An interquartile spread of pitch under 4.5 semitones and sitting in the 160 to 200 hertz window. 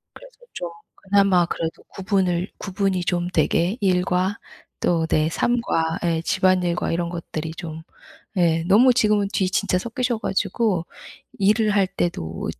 Yes: average, 3.0 semitones; medium, 185 Hz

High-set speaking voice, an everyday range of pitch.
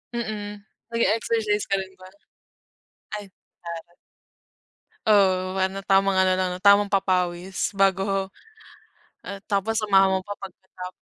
No: high, 195 Hz; narrow, 1.5 semitones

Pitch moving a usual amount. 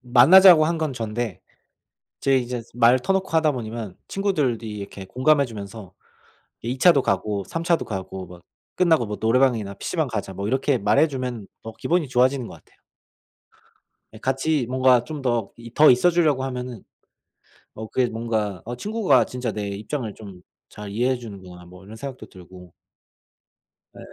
Yes: average, 4.6 semitones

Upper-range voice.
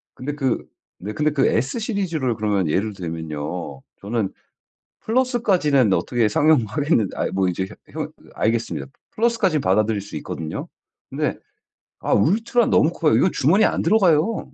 No: low, 130 Hz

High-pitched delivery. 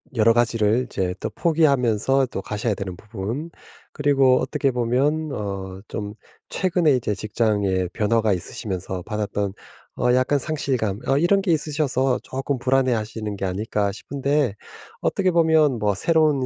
No: low, 120 Hz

